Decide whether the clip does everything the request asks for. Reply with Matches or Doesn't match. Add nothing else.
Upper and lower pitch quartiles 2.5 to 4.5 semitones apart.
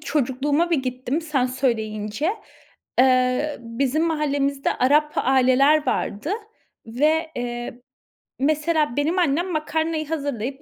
Matches